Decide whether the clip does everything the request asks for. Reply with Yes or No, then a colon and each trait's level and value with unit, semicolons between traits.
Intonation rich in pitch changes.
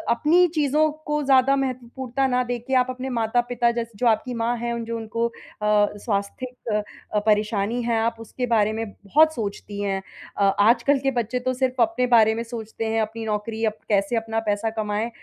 No: narrow, 2.5 semitones